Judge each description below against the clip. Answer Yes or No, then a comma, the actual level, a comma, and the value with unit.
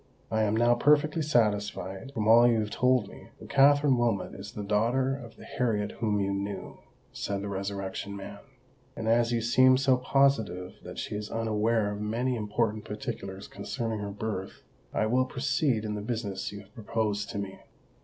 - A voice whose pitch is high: No, low, 110 Hz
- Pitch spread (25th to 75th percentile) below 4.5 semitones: Yes, average, 3.0 semitones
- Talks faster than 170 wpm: Yes, average, 185 wpm